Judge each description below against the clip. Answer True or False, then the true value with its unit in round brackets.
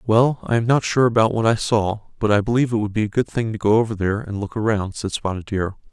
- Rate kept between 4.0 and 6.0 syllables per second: False (6.4 syllables/s)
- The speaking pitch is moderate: False (110 Hz)